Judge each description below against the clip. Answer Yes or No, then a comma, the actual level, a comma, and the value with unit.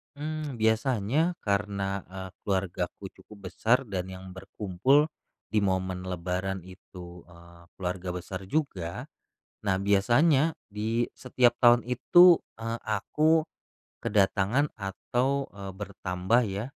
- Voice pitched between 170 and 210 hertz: No, low, 100 Hz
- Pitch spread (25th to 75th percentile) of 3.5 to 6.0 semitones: Yes, average, 4.9 semitones